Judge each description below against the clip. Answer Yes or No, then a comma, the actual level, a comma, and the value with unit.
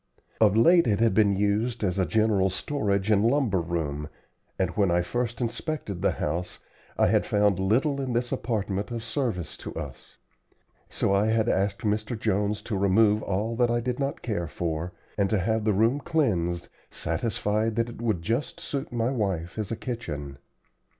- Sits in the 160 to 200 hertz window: No, low, 105 Hz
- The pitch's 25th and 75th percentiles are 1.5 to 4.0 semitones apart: Yes, average, 3.6 semitones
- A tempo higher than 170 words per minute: Yes, average, 180 wpm